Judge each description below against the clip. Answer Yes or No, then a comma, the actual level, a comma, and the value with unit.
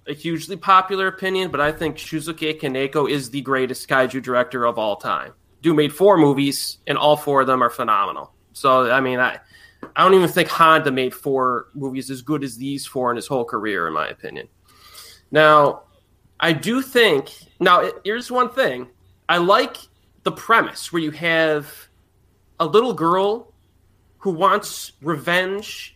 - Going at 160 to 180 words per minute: Yes, average, 170 wpm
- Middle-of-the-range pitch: Yes, medium, 145 Hz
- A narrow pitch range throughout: No, average, 5.1 semitones